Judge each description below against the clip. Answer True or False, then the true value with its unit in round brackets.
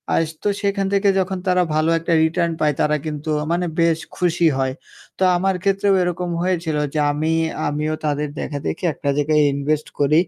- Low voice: False (160 Hz)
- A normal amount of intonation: True (3.1 semitones)